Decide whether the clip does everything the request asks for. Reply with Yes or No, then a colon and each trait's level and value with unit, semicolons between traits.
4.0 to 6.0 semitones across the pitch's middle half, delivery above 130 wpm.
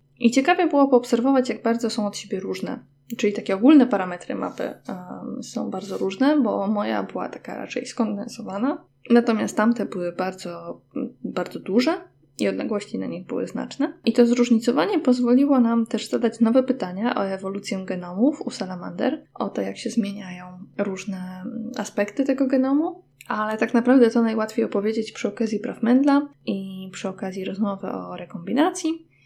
Yes: average, 4.4 semitones; average, 155 wpm